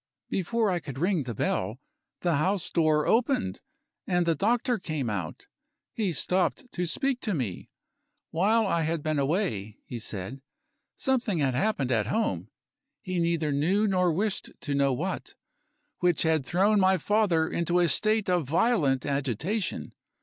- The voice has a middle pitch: Yes, medium, 170 Hz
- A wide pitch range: Yes, wide, 6.2 semitones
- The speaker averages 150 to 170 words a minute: Yes, average, 155 wpm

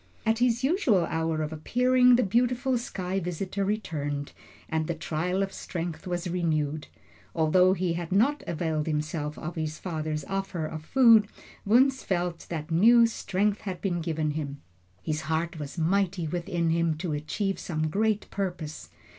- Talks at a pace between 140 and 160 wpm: Yes, average, 155 wpm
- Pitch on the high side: No, medium, 175 Hz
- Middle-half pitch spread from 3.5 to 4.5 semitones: Yes, average, 4.2 semitones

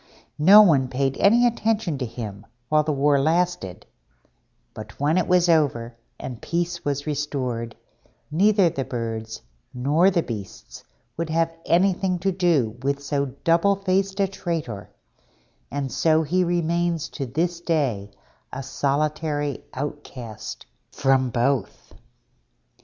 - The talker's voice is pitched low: No, medium, 150 Hz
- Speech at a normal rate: No, slow, 130 wpm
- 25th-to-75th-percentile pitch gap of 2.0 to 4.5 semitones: No, average, 4.9 semitones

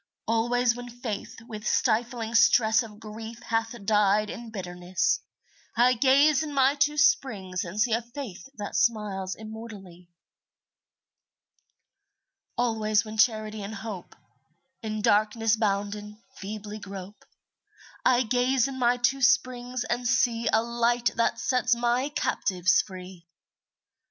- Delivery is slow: Yes, slow, 125 wpm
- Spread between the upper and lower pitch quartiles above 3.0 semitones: No, average, 2.7 semitones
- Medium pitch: No, high, 225 Hz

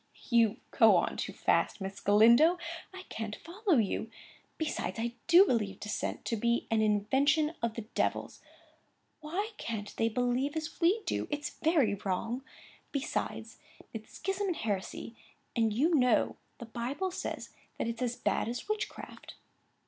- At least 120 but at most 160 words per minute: Yes, average, 150 wpm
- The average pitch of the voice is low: No, high, 240 Hz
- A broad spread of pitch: Yes, wide, 6.2 semitones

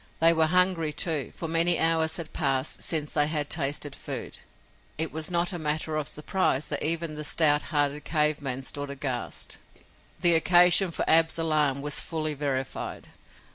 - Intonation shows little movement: Yes, narrow, 2.1 semitones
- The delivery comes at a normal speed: Yes, average, 165 wpm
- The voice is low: No, medium, 155 Hz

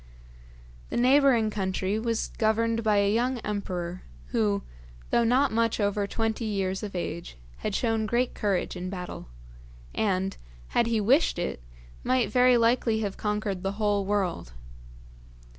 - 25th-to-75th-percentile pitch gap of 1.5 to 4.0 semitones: Yes, average, 2.9 semitones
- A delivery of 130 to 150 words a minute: Yes, average, 140 wpm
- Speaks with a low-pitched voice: No, high, 215 Hz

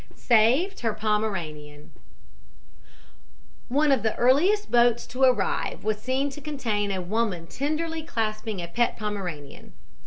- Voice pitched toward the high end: Yes, high, 225 Hz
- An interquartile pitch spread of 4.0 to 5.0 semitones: Yes, average, 4.6 semitones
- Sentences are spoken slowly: Yes, slow, 125 wpm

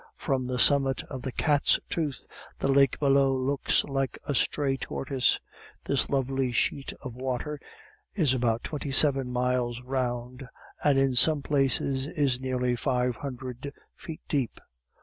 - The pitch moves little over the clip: Yes, narrow, 1.9 semitones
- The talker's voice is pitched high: No, low, 135 Hz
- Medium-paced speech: Yes, average, 145 wpm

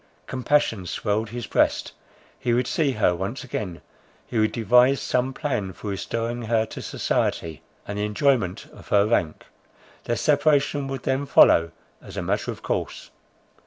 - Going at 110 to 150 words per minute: No, average, 160 wpm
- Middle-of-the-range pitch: No, low, 115 Hz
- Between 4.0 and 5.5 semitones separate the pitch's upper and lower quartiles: Yes, average, 4.4 semitones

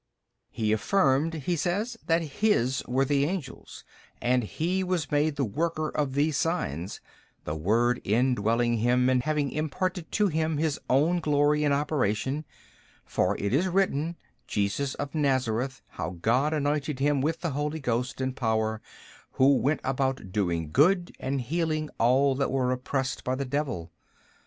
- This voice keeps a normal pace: Yes, average, 155 wpm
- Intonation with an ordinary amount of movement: Yes, average, 3.9 semitones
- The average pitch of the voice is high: No, medium, 140 Hz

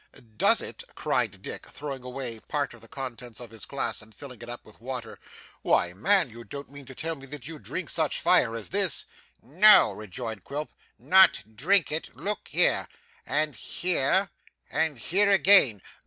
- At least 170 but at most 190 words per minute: Yes, average, 175 wpm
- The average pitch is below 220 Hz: Yes, low, 135 Hz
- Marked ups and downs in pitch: Yes, wide, 5.9 semitones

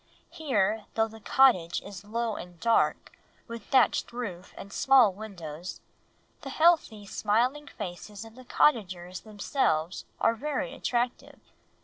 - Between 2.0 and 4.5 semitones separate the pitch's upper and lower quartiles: No, average, 5.1 semitones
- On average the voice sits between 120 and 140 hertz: No, high, 225 Hz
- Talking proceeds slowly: Yes, slow, 125 wpm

